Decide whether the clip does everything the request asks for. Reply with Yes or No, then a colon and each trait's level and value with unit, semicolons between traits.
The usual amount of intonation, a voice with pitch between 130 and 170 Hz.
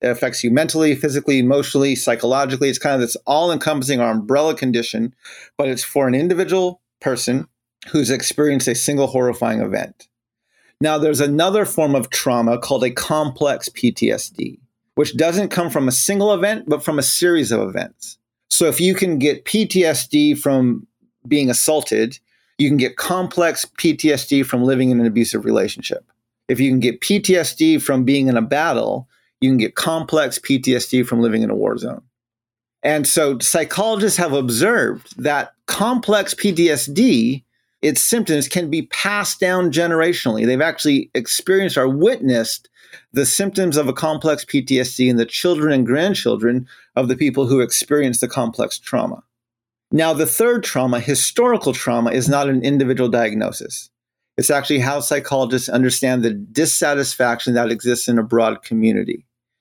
Yes: average, 4.4 semitones; low, 135 Hz